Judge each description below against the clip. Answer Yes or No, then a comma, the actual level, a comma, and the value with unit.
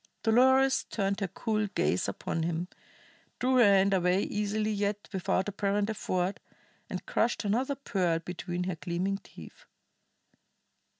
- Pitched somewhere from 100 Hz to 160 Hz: No, high, 200 Hz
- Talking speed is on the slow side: Yes, slow, 130 wpm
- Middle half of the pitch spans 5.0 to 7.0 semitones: No, average, 3.2 semitones